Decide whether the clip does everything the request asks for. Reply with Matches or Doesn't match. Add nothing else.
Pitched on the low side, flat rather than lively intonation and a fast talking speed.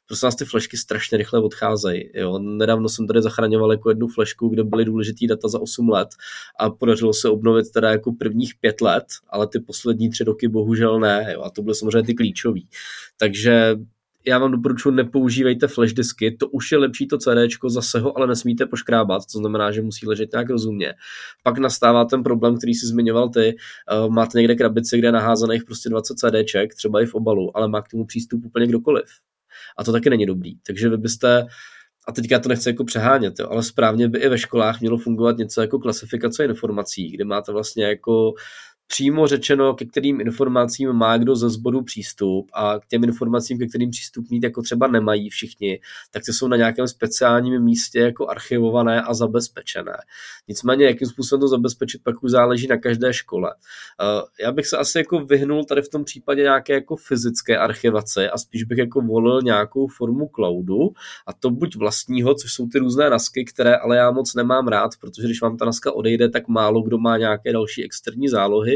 Matches